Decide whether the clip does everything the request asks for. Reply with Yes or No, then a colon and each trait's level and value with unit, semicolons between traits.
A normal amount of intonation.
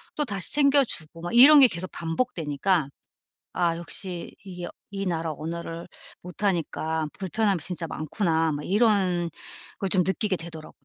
Yes: average, 3.5 semitones